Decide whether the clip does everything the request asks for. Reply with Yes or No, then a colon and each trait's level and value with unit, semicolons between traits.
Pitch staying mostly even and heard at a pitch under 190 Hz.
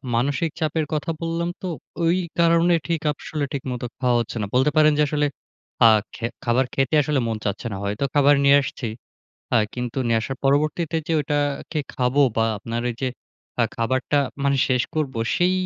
No: average, 3.9 semitones; medium, 140 Hz